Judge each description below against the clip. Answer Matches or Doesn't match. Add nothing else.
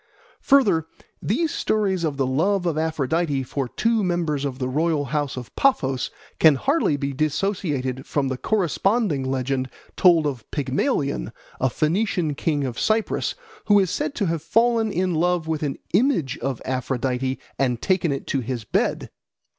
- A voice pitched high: Doesn't match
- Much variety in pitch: Matches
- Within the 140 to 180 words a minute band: Matches